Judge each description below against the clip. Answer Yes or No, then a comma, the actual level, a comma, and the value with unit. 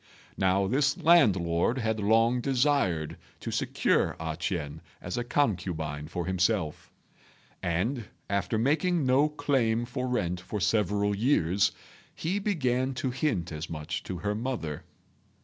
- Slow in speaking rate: Yes, slow, 130 wpm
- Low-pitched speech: Yes, low, 105 Hz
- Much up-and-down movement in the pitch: Yes, wide, 6.8 semitones